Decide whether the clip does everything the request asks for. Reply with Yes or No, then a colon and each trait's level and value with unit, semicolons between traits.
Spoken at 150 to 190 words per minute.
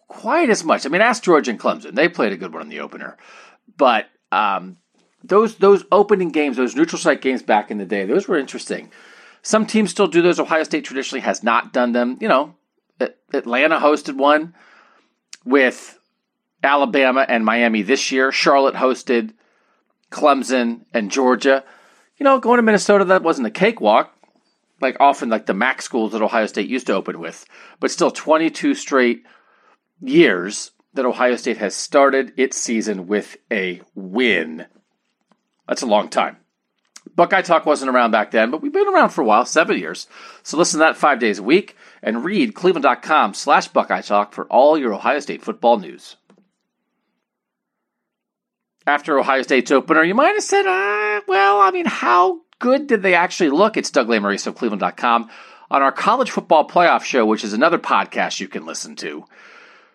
Yes: average, 175 wpm